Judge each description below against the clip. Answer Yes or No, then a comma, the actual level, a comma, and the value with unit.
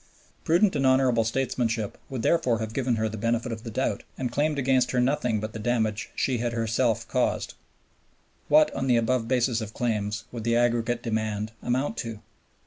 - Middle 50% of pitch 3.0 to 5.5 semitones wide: No, narrow, 2.6 semitones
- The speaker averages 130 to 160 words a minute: No, average, 185 wpm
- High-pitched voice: No, low, 120 Hz